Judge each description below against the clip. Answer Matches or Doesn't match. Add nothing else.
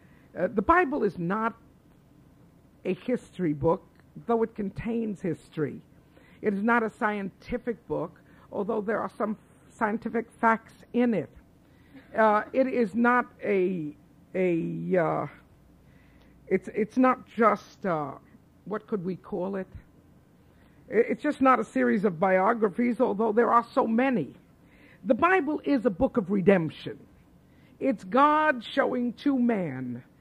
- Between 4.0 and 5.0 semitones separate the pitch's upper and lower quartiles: Matches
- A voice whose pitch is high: Matches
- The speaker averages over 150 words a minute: Doesn't match